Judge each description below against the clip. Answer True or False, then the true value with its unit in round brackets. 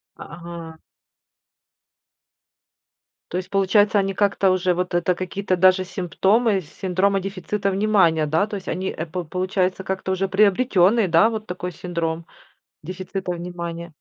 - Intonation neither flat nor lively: False (2.1 semitones)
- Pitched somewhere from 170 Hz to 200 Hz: True (185 Hz)